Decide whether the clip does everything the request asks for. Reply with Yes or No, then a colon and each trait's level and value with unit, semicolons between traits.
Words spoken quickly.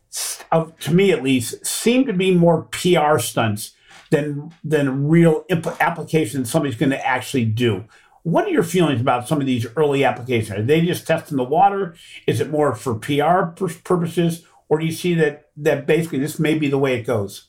No: average, 195 wpm